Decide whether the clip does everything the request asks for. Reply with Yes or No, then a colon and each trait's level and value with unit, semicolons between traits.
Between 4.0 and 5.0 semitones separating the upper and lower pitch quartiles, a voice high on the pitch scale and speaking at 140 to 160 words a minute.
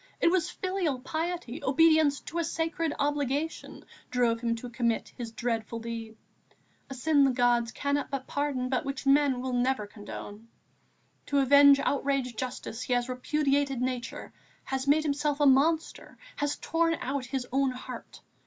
No: average, 2.9 semitones; very high, 275 Hz; average, 155 wpm